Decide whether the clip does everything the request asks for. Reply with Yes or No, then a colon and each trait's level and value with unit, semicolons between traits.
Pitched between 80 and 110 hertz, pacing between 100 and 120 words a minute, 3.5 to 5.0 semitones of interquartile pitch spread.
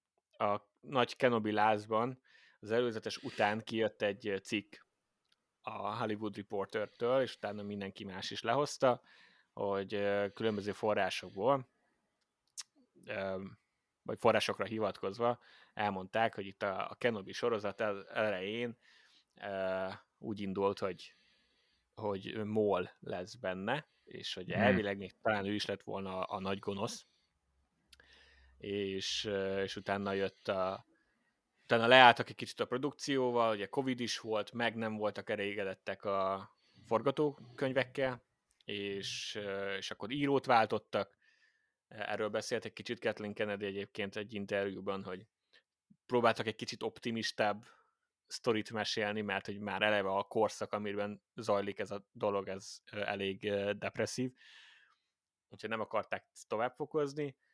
No: low, 105 Hz; average, 115 wpm; average, 2.7 semitones